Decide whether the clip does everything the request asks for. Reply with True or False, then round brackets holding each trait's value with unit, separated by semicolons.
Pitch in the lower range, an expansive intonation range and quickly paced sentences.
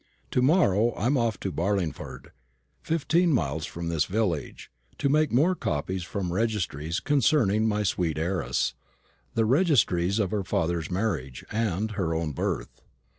False (100 Hz; 5.8 semitones; 150 wpm)